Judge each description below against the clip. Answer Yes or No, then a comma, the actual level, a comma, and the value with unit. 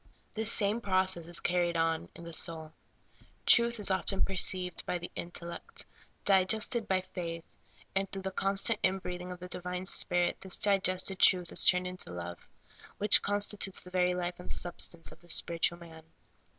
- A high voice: No, medium, 180 Hz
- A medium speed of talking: Yes, average, 175 wpm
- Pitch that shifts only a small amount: Yes, narrow, 2.0 semitones